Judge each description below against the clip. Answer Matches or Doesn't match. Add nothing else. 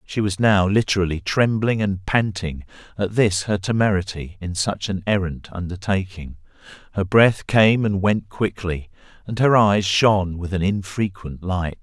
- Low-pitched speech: Matches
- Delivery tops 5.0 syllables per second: Doesn't match